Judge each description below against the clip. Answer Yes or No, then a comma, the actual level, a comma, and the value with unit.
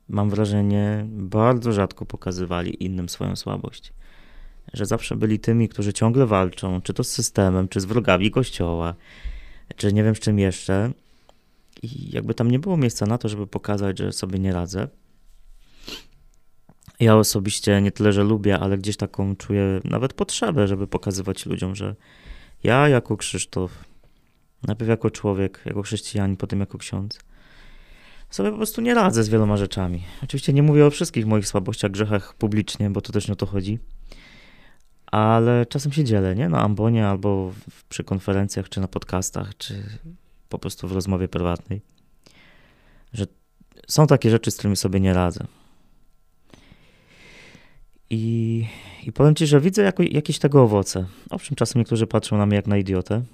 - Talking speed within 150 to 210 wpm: Yes, fast, 160 wpm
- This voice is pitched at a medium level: No, low, 105 Hz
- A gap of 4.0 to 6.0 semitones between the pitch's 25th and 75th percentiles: No, average, 3.0 semitones